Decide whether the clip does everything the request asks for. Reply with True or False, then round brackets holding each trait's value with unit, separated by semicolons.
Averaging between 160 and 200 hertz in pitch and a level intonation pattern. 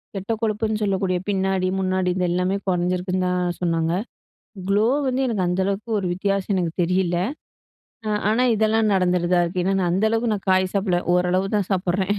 True (190 Hz; 2.0 semitones)